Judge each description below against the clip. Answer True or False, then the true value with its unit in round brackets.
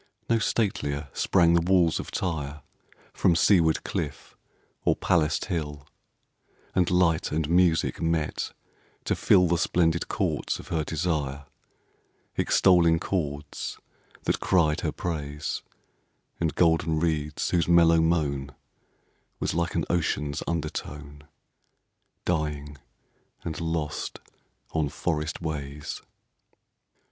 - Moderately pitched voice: False (80 Hz)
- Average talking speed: False (110 wpm)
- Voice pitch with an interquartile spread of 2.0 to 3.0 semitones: True (2.4 semitones)